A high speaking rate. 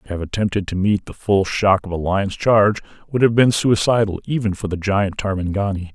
Yes: fast, 210 wpm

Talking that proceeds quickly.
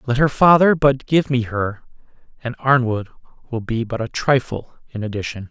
No: average, 175 wpm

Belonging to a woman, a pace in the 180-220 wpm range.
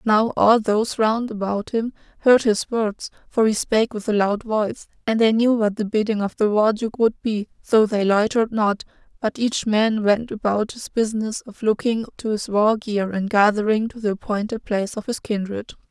Yes: female; fast, 205 wpm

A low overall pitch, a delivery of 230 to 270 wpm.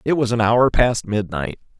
No: low, 115 Hz; average, 200 wpm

